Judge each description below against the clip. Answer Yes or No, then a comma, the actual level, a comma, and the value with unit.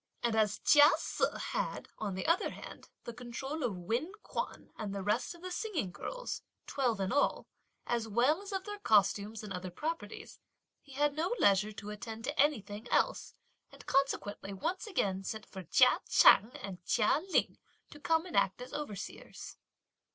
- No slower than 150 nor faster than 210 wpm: Yes, average, 175 wpm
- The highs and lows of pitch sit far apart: Yes, wide, 6.7 semitones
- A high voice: Yes, high, 235 Hz